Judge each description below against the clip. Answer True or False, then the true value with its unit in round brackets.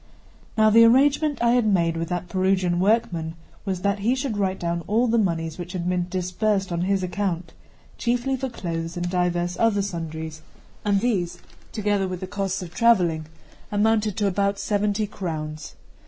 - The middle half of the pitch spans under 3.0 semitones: False (3.6 semitones)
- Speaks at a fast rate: False (170 wpm)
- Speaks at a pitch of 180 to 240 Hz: True (190 Hz)